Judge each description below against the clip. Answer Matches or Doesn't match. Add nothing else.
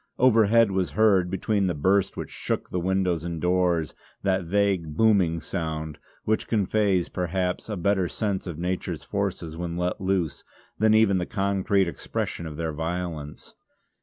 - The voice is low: Matches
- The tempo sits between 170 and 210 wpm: Doesn't match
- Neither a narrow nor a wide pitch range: Matches